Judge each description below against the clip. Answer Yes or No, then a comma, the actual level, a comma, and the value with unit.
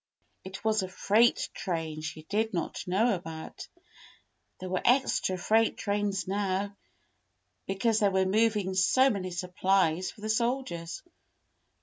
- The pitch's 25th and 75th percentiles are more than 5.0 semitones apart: No, average, 3.0 semitones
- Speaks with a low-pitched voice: No, high, 195 Hz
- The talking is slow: Yes, slow, 130 wpm